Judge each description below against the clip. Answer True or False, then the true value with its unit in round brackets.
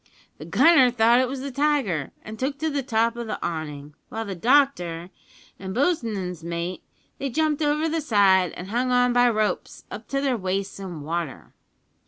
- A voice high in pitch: True (225 Hz)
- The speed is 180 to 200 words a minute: True (185 wpm)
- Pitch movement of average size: False (6.9 semitones)